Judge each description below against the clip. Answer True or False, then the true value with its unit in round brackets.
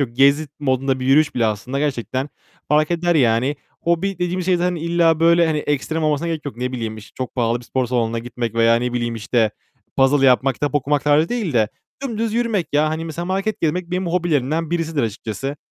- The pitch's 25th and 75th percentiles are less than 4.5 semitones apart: False (5.3 semitones)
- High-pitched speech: False (145 Hz)